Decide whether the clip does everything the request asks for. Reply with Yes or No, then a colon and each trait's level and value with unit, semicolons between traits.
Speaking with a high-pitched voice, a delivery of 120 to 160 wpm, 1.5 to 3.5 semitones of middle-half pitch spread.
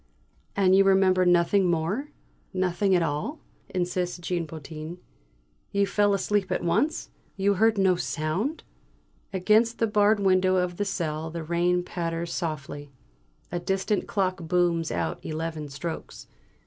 No: medium, 180 Hz; slow, 135 wpm; average, 2.9 semitones